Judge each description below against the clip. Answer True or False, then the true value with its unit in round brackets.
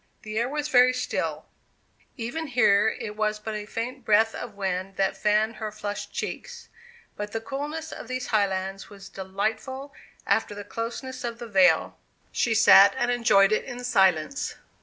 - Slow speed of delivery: False (165 wpm)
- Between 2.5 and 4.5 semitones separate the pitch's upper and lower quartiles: True (3.6 semitones)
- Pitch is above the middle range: True (220 Hz)